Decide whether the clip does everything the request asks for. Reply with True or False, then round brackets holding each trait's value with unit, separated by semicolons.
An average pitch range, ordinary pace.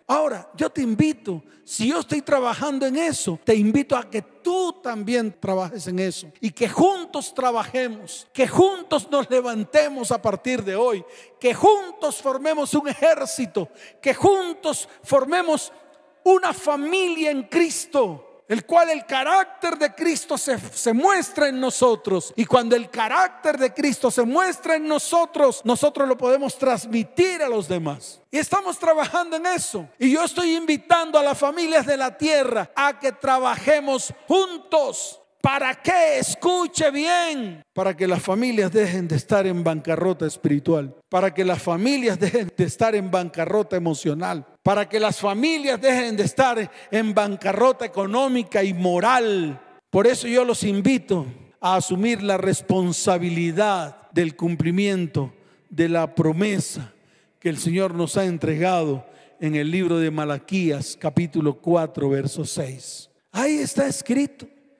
False (7.9 semitones; 145 wpm)